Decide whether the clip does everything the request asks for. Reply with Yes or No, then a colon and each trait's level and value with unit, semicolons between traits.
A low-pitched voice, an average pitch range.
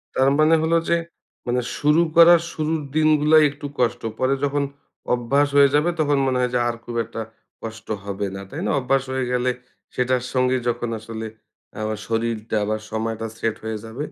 Yes: low, 125 Hz; average, 4.4 semitones